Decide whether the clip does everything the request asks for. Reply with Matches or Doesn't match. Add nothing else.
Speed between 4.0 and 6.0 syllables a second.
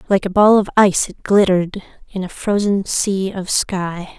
Matches